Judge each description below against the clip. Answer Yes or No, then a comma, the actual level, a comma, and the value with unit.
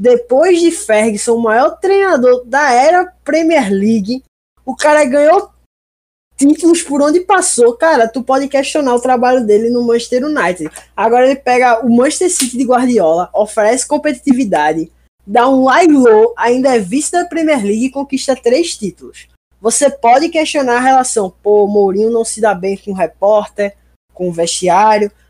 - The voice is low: No, very high, 250 Hz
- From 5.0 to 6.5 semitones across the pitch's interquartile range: Yes, average, 5.3 semitones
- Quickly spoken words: No, average, 160 wpm